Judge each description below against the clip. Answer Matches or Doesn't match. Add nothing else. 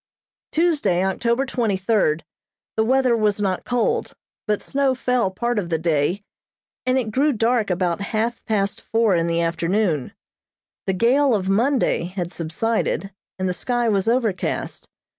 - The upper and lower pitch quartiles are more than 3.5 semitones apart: Matches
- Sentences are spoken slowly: Doesn't match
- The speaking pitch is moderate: Doesn't match